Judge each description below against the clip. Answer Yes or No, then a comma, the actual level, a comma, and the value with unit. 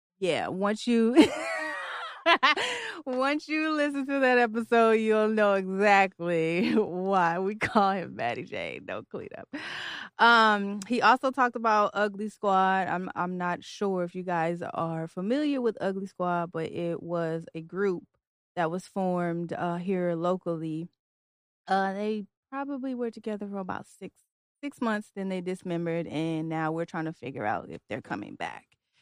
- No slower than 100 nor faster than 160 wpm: Yes, average, 155 wpm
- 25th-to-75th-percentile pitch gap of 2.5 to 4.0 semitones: No, average, 4.6 semitones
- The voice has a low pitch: No, high, 195 Hz